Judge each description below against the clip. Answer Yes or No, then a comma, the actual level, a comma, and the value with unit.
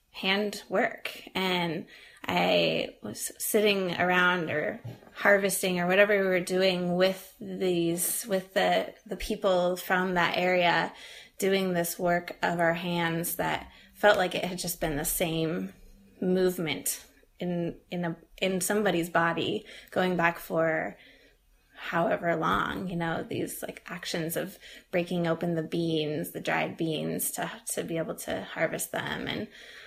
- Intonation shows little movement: Yes, narrow, 2.1 semitones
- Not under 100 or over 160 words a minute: Yes, average, 145 wpm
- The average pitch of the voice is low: No, medium, 180 Hz